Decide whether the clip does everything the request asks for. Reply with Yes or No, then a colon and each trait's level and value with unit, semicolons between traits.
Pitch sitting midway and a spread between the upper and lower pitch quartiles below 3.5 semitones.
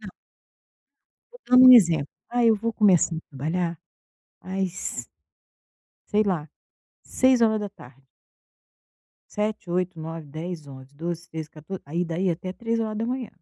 No: medium, 180 Hz; average, 5.2 semitones